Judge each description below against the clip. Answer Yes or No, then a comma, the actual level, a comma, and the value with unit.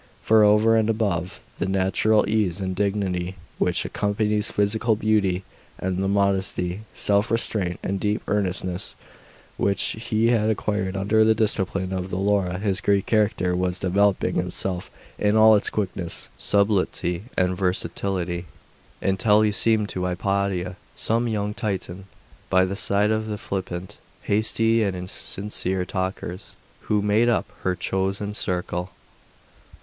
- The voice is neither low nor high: No, low, 100 Hz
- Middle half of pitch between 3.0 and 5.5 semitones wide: No, narrow, 2.4 semitones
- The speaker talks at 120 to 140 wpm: Yes, slow, 135 wpm